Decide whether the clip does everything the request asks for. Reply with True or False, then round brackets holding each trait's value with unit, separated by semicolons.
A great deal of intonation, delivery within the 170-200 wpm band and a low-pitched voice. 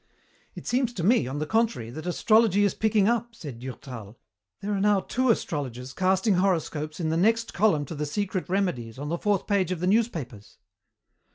False (6.3 semitones; 190 wpm; 185 Hz)